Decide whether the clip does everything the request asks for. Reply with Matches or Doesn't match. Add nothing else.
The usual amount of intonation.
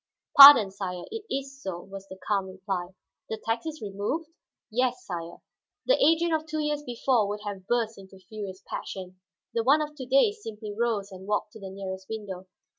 Doesn't match